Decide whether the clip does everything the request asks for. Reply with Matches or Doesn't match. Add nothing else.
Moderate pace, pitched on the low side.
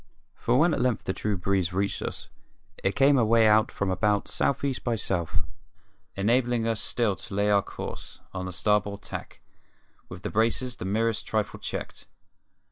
Matches